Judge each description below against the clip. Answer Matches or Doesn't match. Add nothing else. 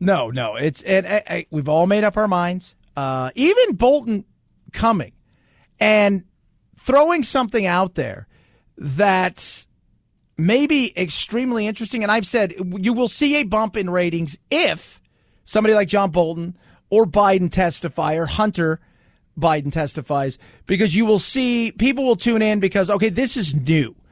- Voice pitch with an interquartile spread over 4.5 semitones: Matches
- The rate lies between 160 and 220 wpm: Doesn't match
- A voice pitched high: Matches